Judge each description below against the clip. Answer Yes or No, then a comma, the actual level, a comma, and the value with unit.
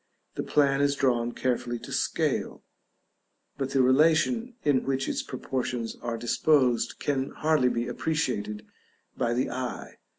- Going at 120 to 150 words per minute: Yes, slow, 135 wpm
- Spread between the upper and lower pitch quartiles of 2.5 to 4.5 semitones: Yes, average, 2.9 semitones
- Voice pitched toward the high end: No, low, 130 Hz